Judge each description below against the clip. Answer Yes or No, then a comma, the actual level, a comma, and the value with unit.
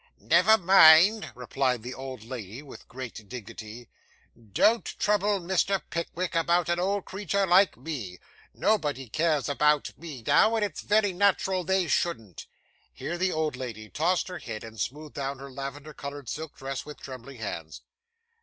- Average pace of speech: Yes, average, 155 wpm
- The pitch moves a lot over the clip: Yes, wide, 6.5 semitones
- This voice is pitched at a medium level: Yes, medium, 150 Hz